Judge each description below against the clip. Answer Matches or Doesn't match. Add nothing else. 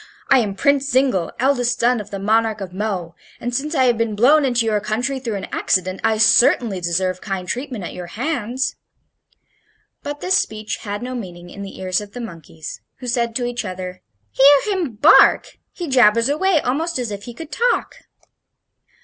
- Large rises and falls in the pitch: Doesn't match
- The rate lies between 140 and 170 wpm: Doesn't match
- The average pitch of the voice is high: Matches